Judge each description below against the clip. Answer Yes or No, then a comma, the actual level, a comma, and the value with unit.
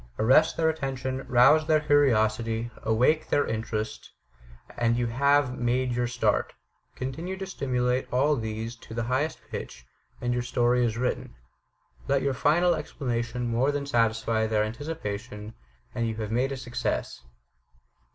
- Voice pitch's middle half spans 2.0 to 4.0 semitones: Yes, average, 3.5 semitones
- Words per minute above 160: No, average, 145 wpm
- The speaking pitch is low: Yes, low, 125 Hz